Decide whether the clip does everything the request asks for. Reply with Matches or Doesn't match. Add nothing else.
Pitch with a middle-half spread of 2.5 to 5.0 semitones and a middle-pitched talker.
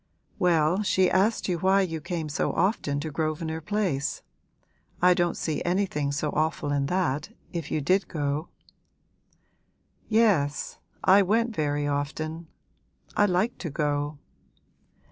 Matches